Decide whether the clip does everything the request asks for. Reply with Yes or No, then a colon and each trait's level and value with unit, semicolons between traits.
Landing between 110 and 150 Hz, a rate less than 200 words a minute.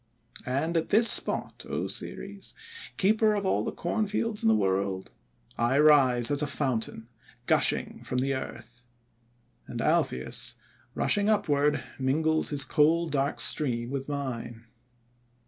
Yes: medium, 140 Hz; slow, 135 wpm